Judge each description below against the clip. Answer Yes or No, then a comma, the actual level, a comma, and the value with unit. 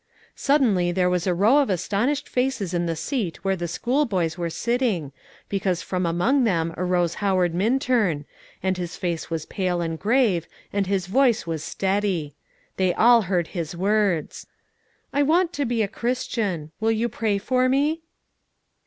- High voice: Yes, high, 195 Hz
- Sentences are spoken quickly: No, average, 160 wpm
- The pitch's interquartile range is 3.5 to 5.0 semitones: No, wide, 5.6 semitones